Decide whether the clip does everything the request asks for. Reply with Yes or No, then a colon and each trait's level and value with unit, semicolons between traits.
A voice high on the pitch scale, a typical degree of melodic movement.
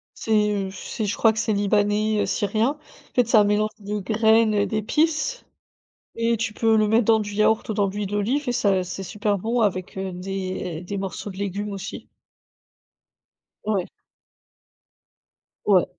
No: high, 210 Hz; narrow, 2.0 semitones